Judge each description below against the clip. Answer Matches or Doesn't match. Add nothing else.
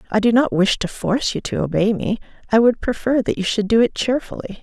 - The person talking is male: Doesn't match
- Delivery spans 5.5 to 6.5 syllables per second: Matches